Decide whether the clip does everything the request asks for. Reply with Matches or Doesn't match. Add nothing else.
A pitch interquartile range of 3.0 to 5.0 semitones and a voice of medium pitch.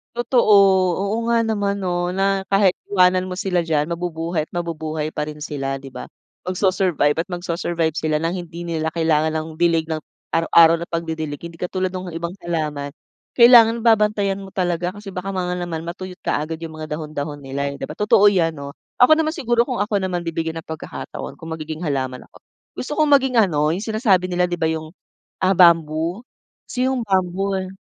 Matches